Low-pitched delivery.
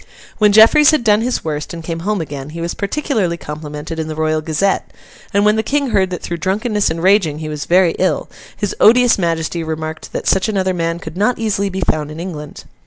No: medium, 180 Hz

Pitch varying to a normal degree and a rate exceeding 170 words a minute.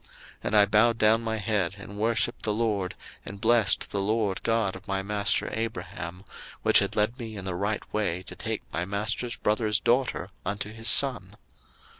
No: narrow, 2.2 semitones; average, 185 wpm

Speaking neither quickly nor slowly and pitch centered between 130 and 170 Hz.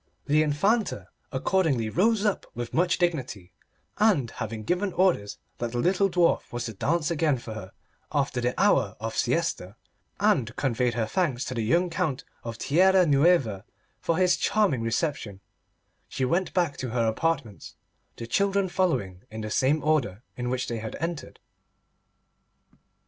Yes: average, 155 wpm; medium, 140 Hz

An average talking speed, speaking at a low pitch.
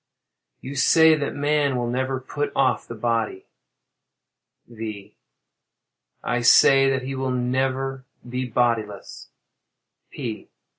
No: slow, 110 wpm; low, 130 Hz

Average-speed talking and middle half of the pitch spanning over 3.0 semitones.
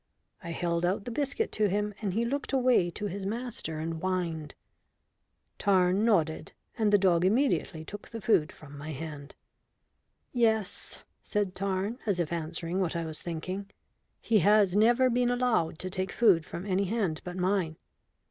Yes: average, 165 wpm; average, 4.3 semitones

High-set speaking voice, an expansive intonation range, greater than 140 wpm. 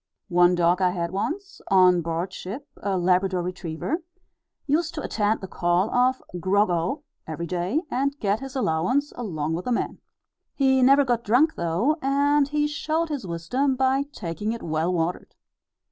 Yes: high, 205 Hz; wide, 7.7 semitones; average, 165 wpm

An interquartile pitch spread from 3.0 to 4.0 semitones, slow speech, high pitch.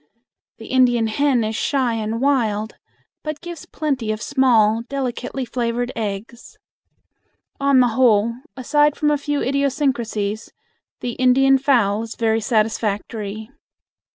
Yes: average, 3.7 semitones; slow, 125 wpm; high, 240 Hz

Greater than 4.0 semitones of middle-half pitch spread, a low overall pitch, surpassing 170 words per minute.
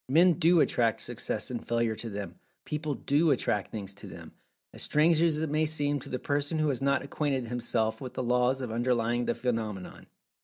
Yes: average, 4.5 semitones; low, 130 Hz; average, 185 wpm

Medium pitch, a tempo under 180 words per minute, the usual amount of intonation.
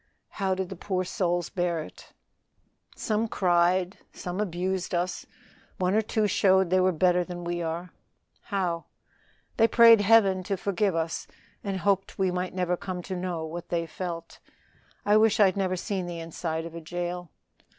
No: medium, 180 Hz; average, 170 wpm; narrow, 1.9 semitones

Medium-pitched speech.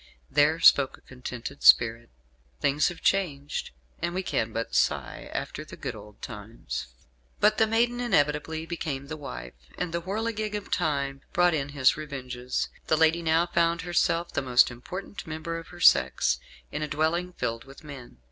Yes: medium, 155 Hz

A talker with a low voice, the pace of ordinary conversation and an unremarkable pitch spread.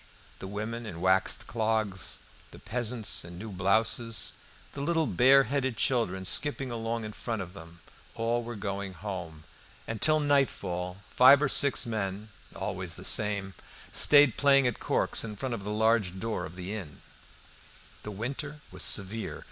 Yes: low, 110 Hz; average, 160 wpm; average, 4.5 semitones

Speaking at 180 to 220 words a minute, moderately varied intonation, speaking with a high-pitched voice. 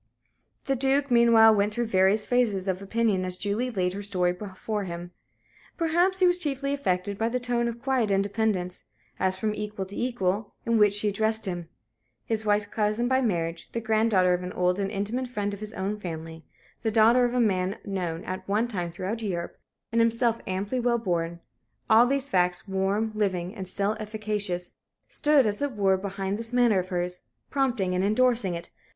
Yes: average, 190 wpm; average, 3.8 semitones; high, 210 Hz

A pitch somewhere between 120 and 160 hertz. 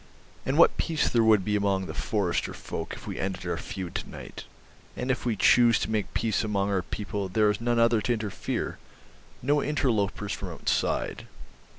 No: low, 105 Hz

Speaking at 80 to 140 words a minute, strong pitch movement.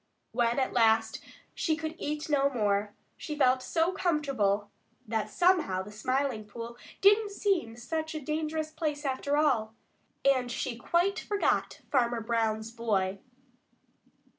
Yes: slow, 135 wpm; wide, 5.7 semitones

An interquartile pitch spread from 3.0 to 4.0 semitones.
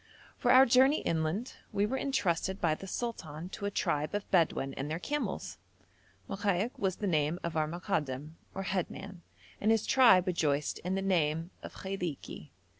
No: average, 4.5 semitones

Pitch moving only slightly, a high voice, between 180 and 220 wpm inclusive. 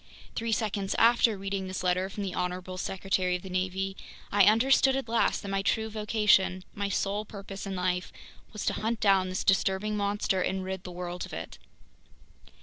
Yes: narrow, 2.3 semitones; high, 195 Hz; average, 185 wpm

